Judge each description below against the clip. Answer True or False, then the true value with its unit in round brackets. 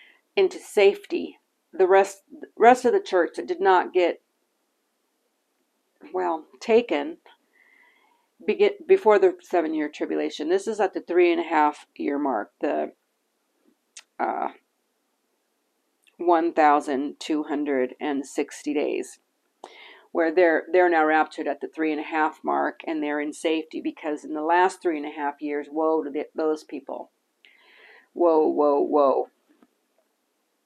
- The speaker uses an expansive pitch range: True (7.9 semitones)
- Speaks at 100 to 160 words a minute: True (140 wpm)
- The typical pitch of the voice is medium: True (170 Hz)